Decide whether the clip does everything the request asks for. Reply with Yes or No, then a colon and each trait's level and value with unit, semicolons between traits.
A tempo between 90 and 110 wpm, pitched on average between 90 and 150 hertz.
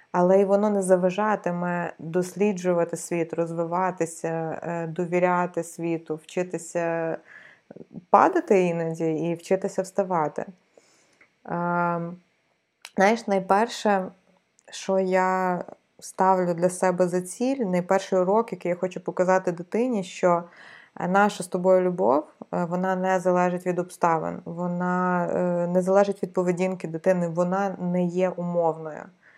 No: slow, 105 wpm; medium, 180 Hz